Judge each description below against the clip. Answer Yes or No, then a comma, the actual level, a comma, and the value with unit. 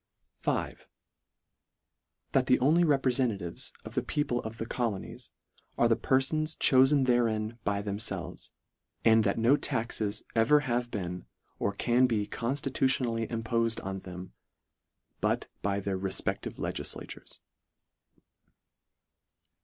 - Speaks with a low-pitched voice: Yes, low, 115 Hz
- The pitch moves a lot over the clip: No, average, 4.1 semitones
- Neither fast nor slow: No, slow, 120 wpm